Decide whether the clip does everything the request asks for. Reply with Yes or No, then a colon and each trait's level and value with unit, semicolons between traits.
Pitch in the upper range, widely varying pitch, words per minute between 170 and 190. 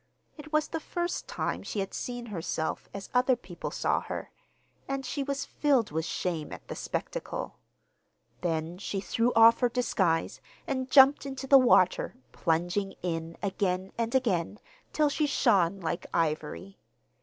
No: high, 210 Hz; wide, 7.3 semitones; average, 155 wpm